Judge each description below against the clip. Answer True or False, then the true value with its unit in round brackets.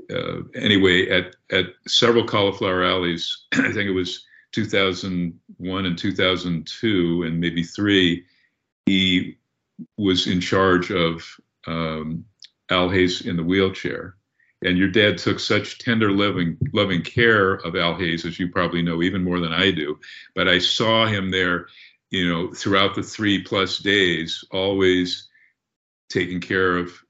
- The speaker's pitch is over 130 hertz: False (90 Hz)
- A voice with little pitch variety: True (1.8 semitones)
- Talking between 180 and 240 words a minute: False (145 wpm)